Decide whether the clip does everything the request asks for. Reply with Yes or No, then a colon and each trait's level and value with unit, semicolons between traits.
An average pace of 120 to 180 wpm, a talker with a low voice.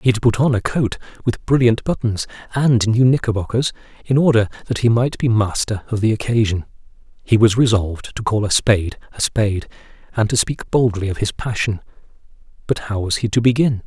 No: average, 190 wpm; low, 115 Hz